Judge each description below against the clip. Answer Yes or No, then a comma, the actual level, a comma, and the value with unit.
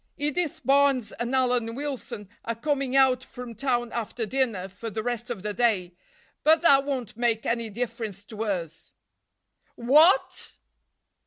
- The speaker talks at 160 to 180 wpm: No, average, 145 wpm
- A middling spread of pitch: Yes, average, 3.6 semitones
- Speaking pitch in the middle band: No, high, 240 Hz